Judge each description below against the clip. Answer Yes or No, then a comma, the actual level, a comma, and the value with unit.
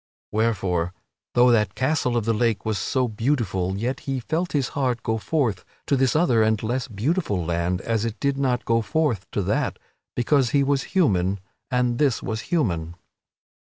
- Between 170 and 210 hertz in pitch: No, low, 115 Hz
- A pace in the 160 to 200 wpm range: Yes, average, 175 wpm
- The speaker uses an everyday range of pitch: Yes, average, 4.6 semitones